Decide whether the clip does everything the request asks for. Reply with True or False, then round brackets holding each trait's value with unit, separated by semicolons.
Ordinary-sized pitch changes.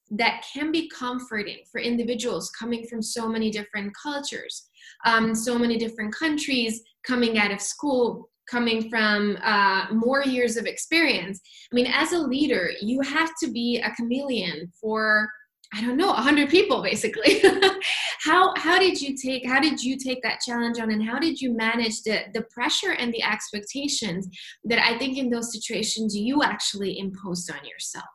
True (4.3 semitones)